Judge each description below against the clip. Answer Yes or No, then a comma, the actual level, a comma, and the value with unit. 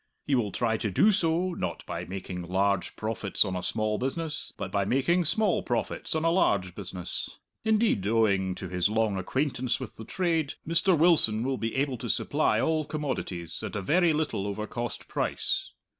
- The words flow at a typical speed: Yes, average, 185 wpm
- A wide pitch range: Yes, wide, 8.2 semitones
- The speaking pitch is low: Yes, low, 115 Hz